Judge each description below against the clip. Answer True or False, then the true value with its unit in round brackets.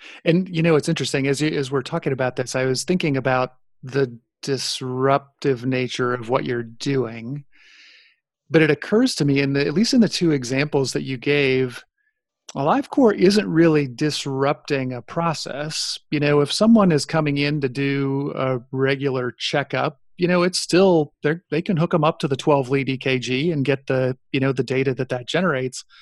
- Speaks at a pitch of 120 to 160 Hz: True (140 Hz)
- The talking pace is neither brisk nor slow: True (190 wpm)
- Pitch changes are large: False (3.8 semitones)